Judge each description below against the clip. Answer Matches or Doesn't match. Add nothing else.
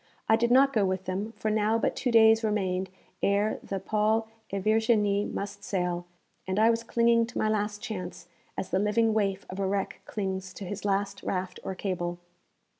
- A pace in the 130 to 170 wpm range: Doesn't match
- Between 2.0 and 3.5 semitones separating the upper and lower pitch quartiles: Matches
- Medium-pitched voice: Doesn't match